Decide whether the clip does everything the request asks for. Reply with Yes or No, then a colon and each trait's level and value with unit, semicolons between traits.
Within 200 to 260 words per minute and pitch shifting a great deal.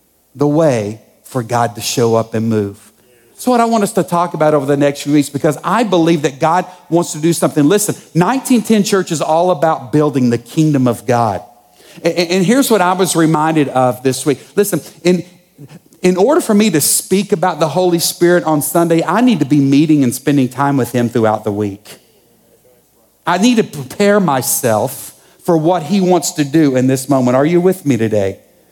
Yes: fast, 205 wpm; wide, 5.7 semitones